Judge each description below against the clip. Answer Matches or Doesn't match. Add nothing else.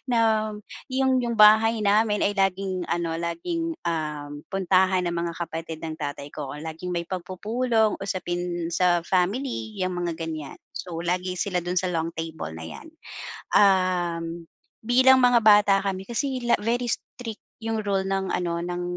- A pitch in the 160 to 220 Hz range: Matches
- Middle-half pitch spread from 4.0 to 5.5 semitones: Matches